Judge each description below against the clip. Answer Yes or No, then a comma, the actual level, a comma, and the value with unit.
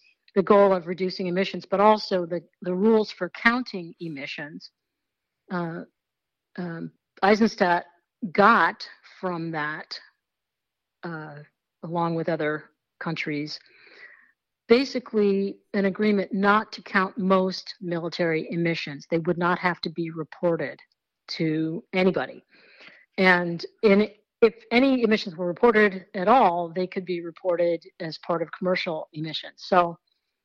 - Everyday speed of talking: No, slow, 120 wpm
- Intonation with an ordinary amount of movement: Yes, average, 3.1 semitones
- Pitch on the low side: No, medium, 180 Hz